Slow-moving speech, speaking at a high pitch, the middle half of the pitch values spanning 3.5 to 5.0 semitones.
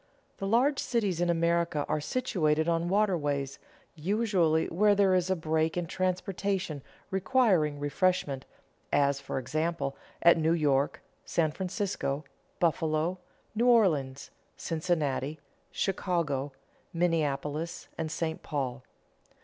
No: slow, 110 wpm; medium, 165 Hz; average, 3.8 semitones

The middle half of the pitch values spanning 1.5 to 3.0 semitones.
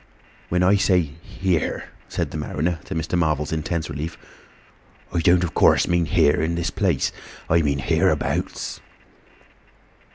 Yes: narrow, 2.4 semitones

